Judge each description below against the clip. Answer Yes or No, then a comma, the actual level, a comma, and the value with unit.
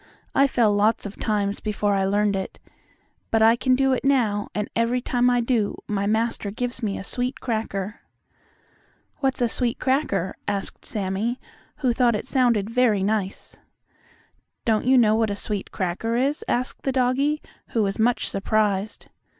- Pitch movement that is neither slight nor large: Yes, average, 3.4 semitones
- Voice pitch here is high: Yes, high, 225 Hz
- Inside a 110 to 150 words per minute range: No, average, 165 wpm